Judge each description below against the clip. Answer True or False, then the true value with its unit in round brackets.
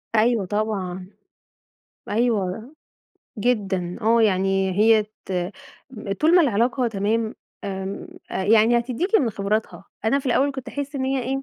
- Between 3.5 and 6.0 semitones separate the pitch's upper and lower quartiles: True (4.2 semitones)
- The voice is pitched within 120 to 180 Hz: False (225 Hz)